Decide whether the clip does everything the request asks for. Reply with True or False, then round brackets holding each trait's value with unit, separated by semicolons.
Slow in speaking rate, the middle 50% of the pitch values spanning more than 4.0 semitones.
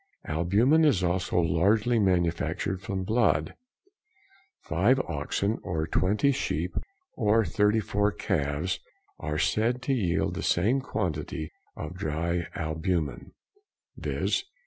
True (105 wpm; 5.0 semitones)